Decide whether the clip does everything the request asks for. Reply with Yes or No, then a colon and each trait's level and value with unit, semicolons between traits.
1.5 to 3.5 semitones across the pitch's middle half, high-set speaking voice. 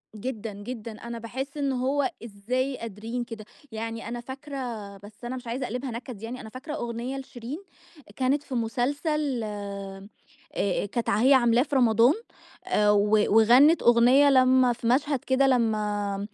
Yes: average, 3.2 semitones; high, 240 Hz